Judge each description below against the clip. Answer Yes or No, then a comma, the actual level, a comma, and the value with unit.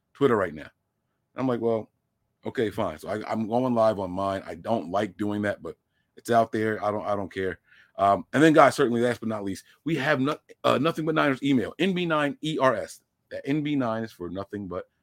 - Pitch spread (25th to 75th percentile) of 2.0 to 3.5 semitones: No, average, 4.7 semitones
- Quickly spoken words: Yes, fast, 215 wpm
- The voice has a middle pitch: No, low, 110 Hz